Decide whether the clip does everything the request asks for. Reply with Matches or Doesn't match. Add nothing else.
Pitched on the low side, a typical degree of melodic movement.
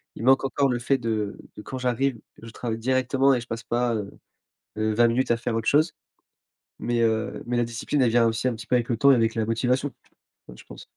Doesn't match